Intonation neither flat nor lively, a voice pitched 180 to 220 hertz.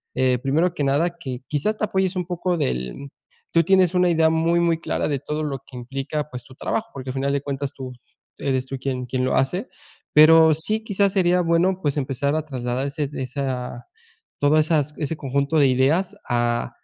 No: average, 4.3 semitones; medium, 145 Hz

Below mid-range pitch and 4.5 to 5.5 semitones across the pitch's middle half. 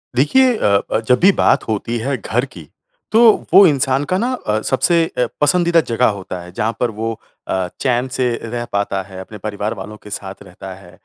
Yes: low, 120 Hz; average, 5.2 semitones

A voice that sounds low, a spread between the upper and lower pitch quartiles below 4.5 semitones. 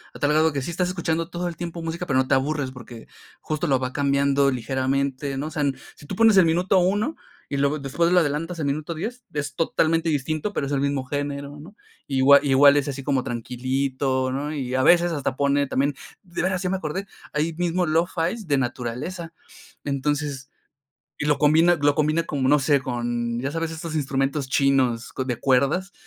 No: medium, 145 Hz; average, 3.5 semitones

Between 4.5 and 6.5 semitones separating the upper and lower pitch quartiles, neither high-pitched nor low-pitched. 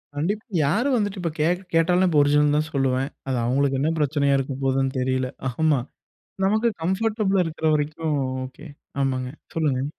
Yes: average, 4.8 semitones; medium, 150 Hz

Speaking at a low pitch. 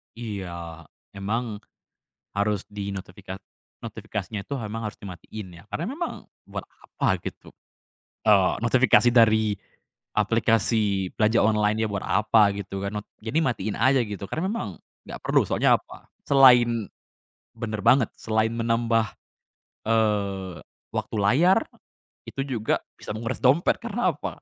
Yes: low, 110 Hz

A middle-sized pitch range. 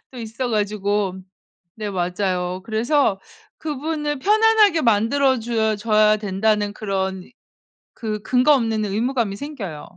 Yes: average, 4.4 semitones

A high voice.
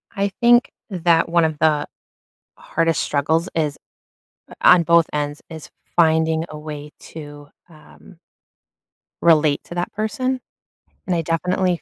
No: medium, 165 Hz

